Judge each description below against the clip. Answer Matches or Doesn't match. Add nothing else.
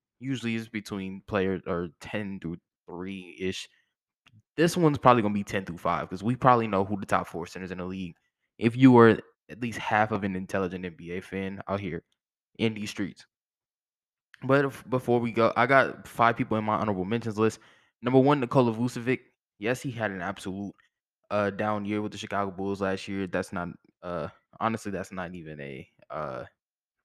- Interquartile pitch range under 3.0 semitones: Doesn't match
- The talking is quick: Doesn't match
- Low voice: Matches